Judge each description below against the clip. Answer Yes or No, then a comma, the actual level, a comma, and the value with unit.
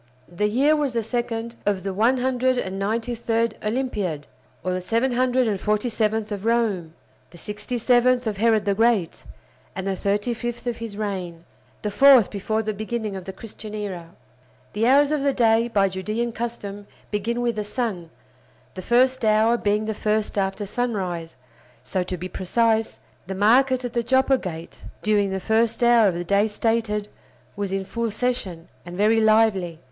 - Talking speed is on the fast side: No, average, 165 wpm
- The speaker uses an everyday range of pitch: Yes, average, 3.3 semitones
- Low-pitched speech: No, high, 215 Hz